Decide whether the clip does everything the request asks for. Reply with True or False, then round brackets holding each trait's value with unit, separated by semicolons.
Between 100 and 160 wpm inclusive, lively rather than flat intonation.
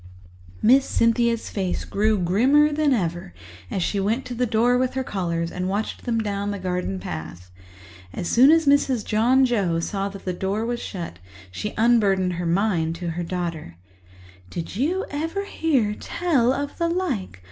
False (170 wpm; 6.1 semitones)